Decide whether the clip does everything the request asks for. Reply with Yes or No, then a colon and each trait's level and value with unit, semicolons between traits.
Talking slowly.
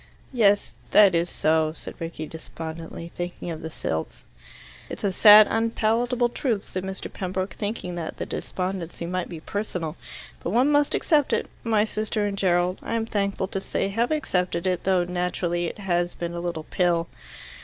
No: average, 175 wpm